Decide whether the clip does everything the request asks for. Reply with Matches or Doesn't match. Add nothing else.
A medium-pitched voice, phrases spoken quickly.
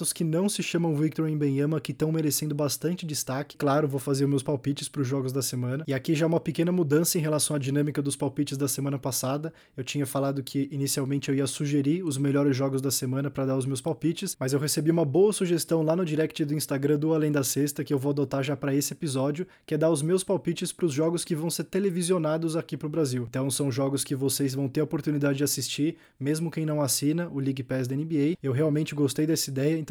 Matches